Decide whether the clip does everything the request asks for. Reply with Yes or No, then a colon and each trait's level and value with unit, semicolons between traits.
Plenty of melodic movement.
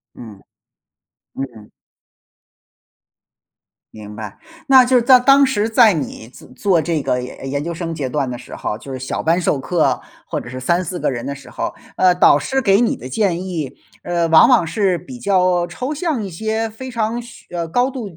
Yes: wide, 8.5 semitones